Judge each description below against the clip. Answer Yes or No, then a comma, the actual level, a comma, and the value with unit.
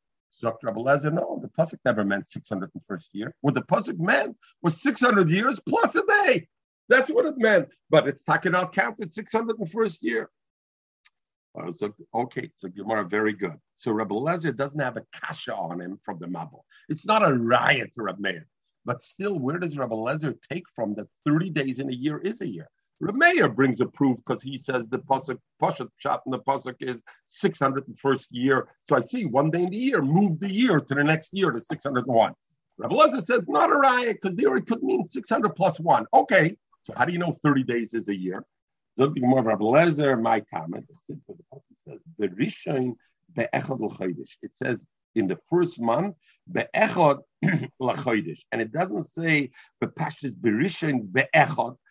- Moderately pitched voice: Yes, medium, 145 Hz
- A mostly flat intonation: No, wide, 7.2 semitones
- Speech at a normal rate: Yes, average, 185 wpm